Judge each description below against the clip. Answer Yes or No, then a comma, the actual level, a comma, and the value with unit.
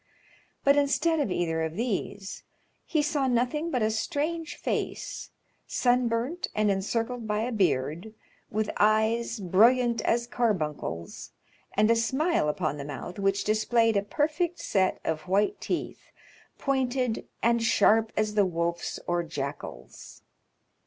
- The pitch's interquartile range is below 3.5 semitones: No, average, 4.9 semitones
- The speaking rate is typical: No, slow, 130 wpm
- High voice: Yes, high, 220 Hz